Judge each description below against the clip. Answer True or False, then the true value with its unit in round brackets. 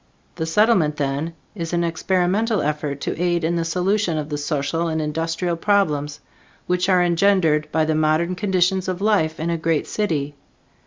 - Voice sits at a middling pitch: True (165 Hz)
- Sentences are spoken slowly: False (170 wpm)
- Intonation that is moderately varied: True (3.0 semitones)